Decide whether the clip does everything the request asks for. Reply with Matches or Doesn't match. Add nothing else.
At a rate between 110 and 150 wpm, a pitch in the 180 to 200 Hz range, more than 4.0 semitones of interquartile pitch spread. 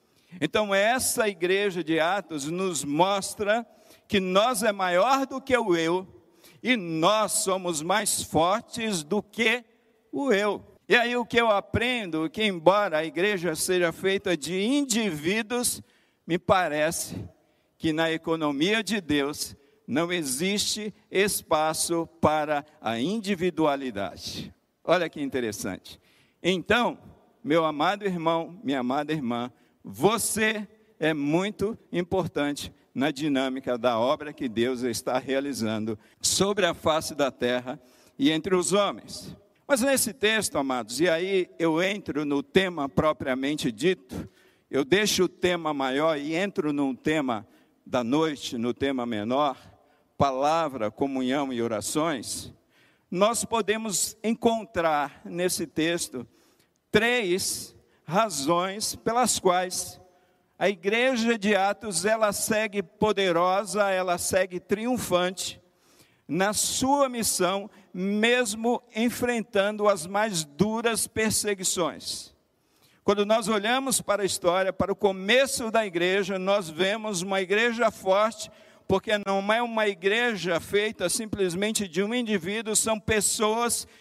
Matches